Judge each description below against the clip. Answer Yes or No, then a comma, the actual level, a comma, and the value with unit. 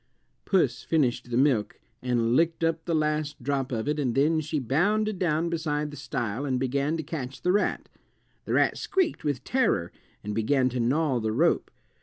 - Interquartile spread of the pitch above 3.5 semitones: Yes, average, 4.5 semitones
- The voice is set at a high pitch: No, medium, 145 Hz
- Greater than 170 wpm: Yes, average, 185 wpm